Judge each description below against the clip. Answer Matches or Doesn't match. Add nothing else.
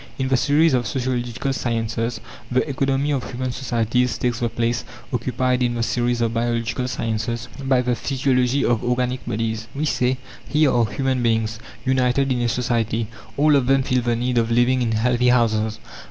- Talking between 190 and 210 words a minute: Doesn't match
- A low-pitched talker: Matches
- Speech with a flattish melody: Matches